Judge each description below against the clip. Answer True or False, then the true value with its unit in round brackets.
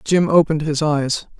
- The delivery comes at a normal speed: True (170 wpm)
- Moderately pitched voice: True (155 Hz)